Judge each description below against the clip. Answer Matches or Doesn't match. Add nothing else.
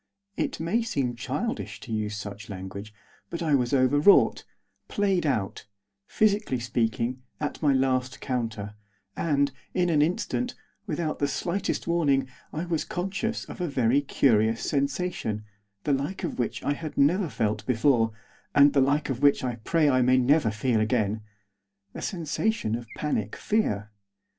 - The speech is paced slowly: Doesn't match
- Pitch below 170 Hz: Matches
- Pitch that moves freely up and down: Matches